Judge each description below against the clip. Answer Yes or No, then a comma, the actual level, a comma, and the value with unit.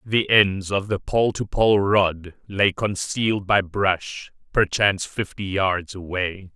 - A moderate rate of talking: Yes, average, 145 wpm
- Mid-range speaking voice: No, low, 100 Hz